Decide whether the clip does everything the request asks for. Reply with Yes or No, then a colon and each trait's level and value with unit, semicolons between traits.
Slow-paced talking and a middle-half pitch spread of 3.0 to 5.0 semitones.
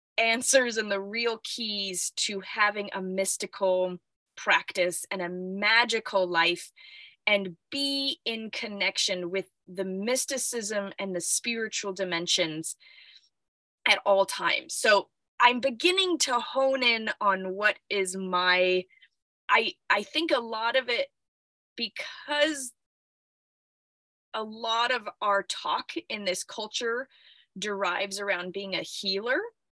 Yes: slow, 120 wpm; average, 4.1 semitones